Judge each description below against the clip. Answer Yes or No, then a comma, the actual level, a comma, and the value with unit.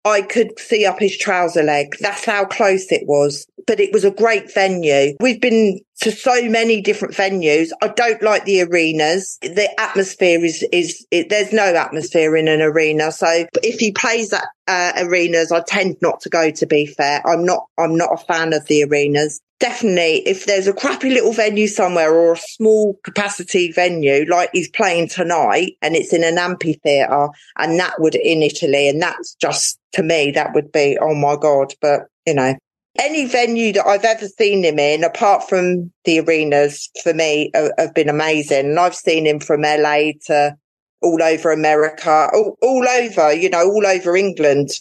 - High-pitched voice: No, medium, 175 Hz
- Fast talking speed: No, average, 190 wpm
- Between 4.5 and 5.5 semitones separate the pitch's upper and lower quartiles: Yes, average, 4.8 semitones